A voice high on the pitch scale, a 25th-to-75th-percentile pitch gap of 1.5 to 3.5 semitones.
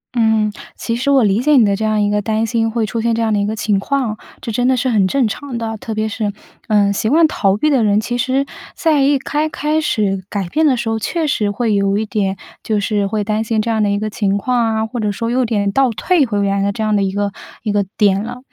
Yes: high, 220 Hz; average, 3.1 semitones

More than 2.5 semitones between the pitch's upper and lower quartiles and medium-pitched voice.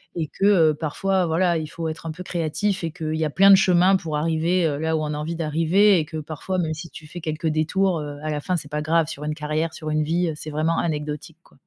No: narrow, 2.2 semitones; medium, 160 Hz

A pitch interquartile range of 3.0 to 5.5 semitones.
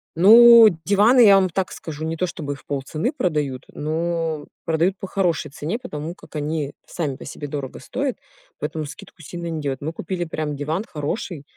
Yes: average, 4.1 semitones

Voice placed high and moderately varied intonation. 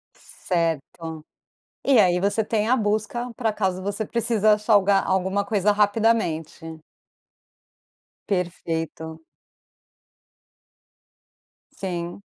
Yes: high, 200 Hz; average, 3.9 semitones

